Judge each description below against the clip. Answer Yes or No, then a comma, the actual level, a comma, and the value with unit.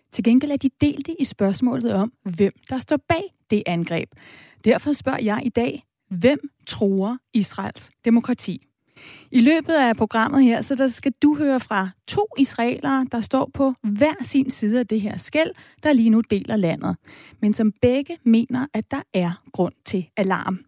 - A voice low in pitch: No, high, 240 Hz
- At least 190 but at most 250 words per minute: No, average, 175 wpm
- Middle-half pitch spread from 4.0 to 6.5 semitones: Yes, average, 4.4 semitones